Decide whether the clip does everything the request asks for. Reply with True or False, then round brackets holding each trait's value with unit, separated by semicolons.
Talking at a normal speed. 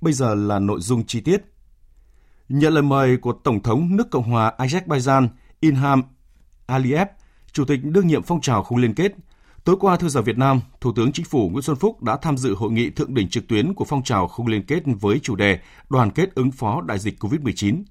True (220 wpm)